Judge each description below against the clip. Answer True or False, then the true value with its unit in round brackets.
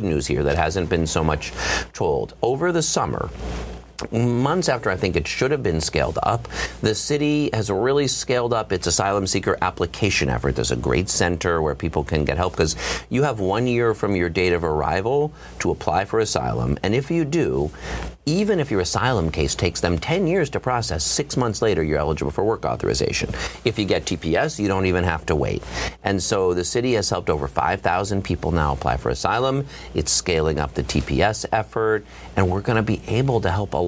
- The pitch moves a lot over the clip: True (6.8 semitones)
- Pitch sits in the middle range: False (95 Hz)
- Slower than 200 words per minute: False (205 wpm)